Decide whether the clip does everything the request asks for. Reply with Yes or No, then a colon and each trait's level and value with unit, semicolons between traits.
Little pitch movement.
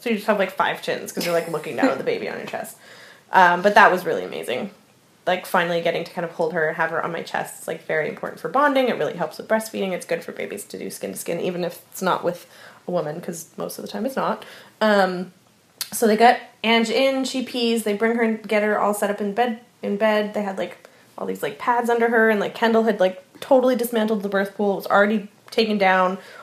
No: average, 4.0 semitones